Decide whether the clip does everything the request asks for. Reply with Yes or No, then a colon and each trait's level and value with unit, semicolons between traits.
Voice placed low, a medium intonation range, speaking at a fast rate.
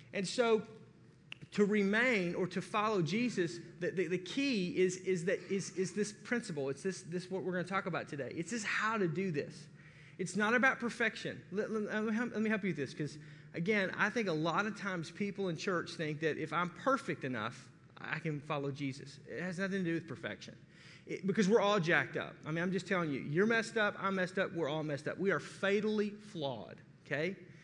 No: medium, 185 Hz; average, 4.6 semitones; fast, 230 wpm